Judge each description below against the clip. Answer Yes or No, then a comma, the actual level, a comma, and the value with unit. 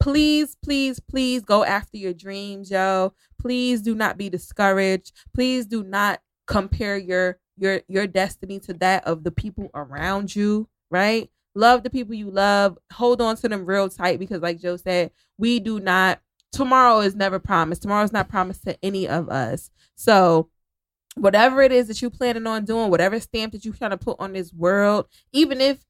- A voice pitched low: No, high, 200 Hz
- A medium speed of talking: Yes, average, 190 wpm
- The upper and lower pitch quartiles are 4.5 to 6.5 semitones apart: No, average, 3.5 semitones